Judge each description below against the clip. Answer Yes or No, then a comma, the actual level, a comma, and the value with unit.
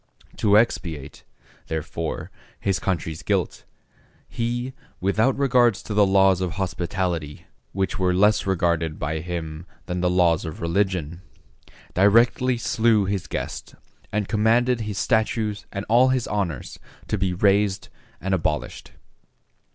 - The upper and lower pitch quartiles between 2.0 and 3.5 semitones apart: No, average, 4.0 semitones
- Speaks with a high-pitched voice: No, very low, 95 Hz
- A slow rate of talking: Yes, slow, 130 wpm